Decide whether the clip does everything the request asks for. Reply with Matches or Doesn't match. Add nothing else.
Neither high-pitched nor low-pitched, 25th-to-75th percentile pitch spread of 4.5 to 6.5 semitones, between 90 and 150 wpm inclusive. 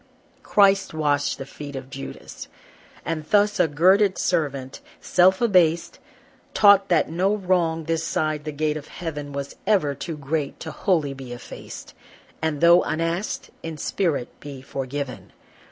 Doesn't match